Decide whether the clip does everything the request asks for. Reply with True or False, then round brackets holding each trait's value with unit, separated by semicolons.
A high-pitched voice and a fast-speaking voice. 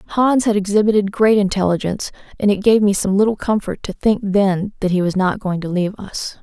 True (200 Hz; 215 wpm)